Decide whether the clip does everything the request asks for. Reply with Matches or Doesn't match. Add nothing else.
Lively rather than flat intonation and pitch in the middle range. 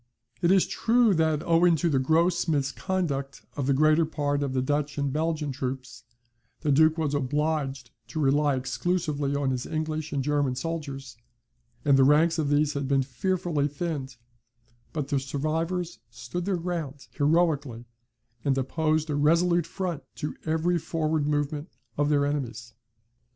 Doesn't match